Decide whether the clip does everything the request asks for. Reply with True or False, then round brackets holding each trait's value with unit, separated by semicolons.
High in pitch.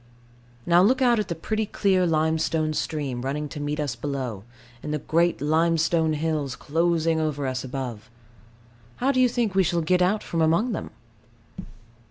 False (160 Hz)